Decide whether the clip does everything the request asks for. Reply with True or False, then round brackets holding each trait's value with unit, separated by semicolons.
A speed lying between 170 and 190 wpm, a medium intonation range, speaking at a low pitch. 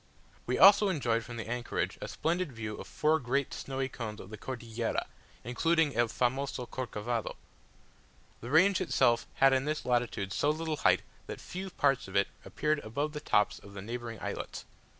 True (175 wpm; 4.7 semitones; 125 Hz)